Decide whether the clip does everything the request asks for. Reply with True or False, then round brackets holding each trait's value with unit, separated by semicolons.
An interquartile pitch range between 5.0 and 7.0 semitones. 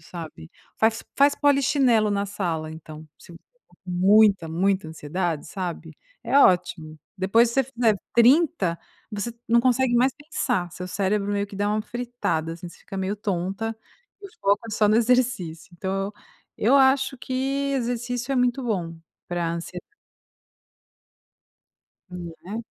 True (5.5 semitones)